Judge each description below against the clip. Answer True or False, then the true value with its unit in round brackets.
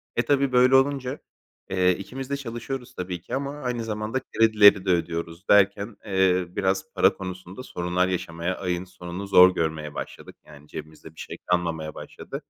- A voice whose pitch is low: True (95 Hz)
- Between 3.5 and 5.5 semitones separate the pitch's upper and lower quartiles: True (5.2 semitones)